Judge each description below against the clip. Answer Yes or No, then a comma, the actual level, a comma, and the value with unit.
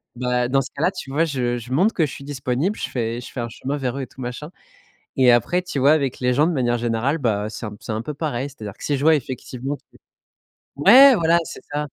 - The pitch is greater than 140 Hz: No, low, 135 Hz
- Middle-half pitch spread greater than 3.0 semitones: Yes, average, 3.6 semitones